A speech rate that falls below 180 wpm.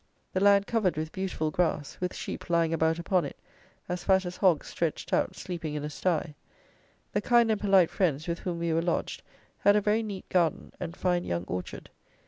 No: average, 200 wpm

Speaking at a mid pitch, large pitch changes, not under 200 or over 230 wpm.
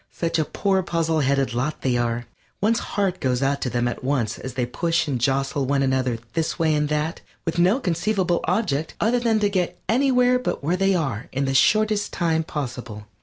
Yes: medium, 155 Hz; wide, 6.2 semitones; fast, 205 wpm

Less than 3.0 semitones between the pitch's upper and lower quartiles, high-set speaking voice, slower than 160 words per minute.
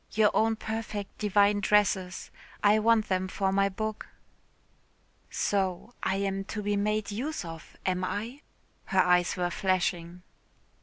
Yes: narrow, 2.4 semitones; high, 200 Hz; average, 140 wpm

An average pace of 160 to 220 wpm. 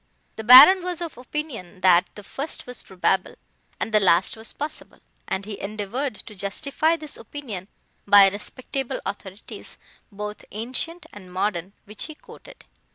No: average, 150 wpm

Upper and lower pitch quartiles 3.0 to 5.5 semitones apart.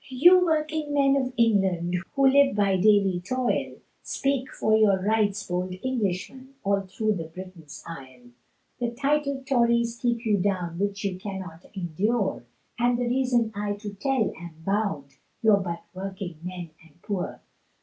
Yes: average, 5.1 semitones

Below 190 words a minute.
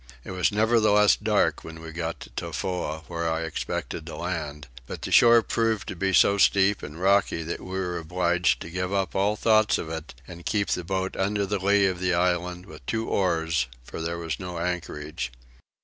No: average, 200 wpm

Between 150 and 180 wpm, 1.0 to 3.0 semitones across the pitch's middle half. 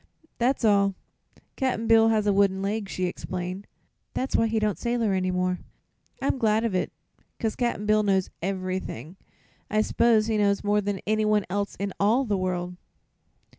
Yes: average, 170 wpm; average, 2.7 semitones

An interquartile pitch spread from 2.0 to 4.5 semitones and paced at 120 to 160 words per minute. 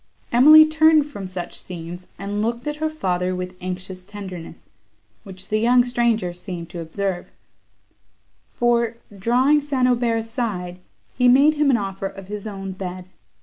No: average, 5.1 semitones; average, 150 wpm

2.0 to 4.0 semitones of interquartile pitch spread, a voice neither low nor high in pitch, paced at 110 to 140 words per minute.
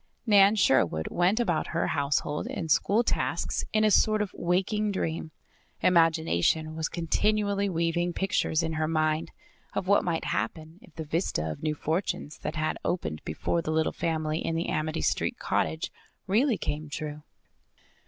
No: average, 3.6 semitones; medium, 165 Hz; average, 160 wpm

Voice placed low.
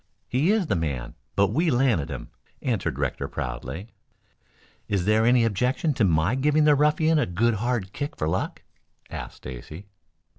Yes: low, 115 Hz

